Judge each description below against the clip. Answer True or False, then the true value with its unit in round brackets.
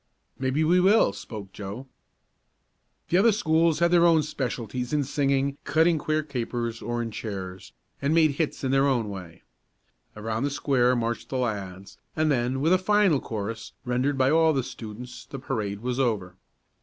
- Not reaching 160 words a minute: False (170 wpm)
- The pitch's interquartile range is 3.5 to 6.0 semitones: True (5.4 semitones)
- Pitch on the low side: True (130 Hz)